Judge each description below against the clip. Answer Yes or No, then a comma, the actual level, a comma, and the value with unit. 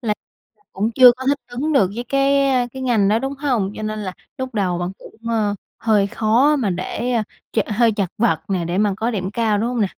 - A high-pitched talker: Yes, high, 220 Hz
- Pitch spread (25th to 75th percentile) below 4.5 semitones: Yes, average, 3.8 semitones